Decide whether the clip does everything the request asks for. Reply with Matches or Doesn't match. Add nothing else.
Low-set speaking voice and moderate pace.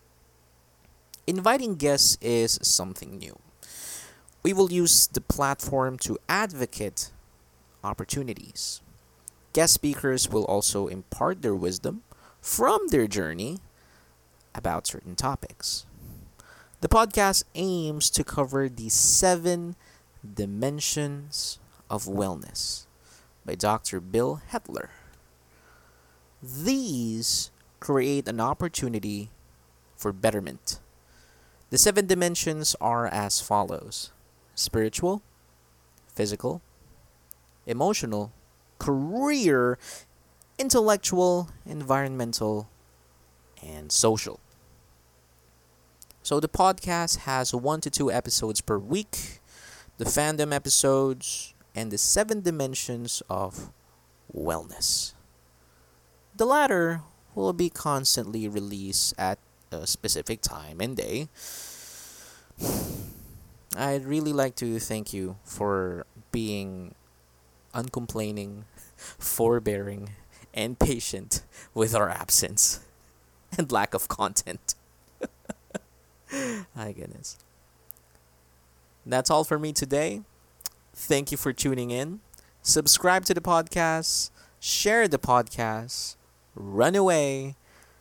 Doesn't match